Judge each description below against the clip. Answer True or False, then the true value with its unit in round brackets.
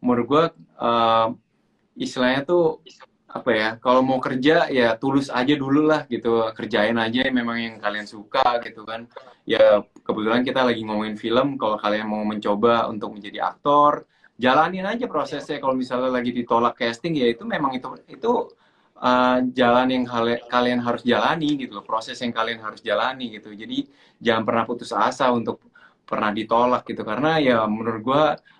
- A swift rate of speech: True (160 wpm)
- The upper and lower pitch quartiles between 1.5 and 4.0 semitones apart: True (2.7 semitones)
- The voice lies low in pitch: True (120 Hz)